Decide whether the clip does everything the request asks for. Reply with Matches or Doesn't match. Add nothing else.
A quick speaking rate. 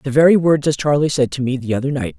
Matches